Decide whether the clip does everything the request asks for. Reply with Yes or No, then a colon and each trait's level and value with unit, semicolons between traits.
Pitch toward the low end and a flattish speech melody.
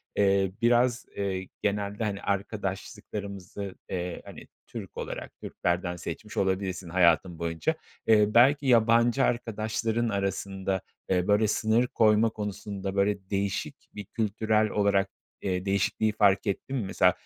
Yes: low, 100 Hz; narrow, 2.3 semitones